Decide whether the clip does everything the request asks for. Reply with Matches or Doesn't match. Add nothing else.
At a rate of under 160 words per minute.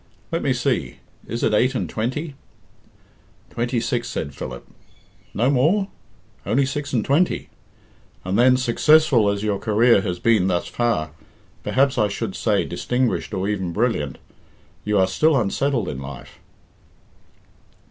Matches